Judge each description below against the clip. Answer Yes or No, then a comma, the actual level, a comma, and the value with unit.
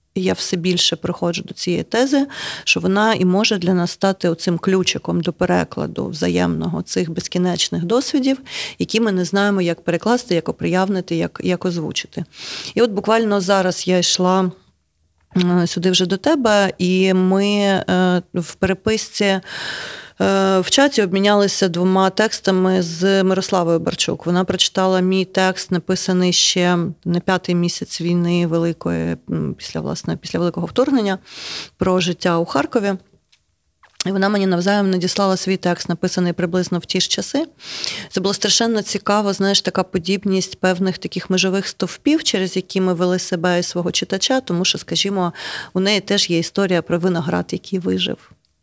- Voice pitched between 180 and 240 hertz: Yes, medium, 185 Hz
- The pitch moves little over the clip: Yes, narrow, 2.0 semitones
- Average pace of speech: Yes, average, 145 wpm